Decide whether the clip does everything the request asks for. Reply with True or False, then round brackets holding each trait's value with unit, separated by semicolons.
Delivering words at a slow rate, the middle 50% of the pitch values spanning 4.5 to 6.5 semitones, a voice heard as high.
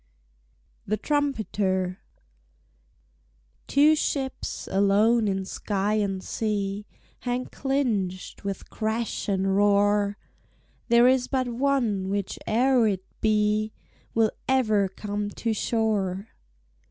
False (95 wpm; 3.2 semitones; 210 Hz)